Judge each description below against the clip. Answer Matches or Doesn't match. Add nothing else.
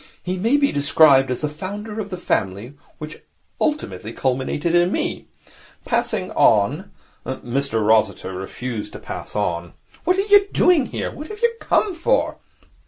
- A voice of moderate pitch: Matches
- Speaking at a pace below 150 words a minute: Doesn't match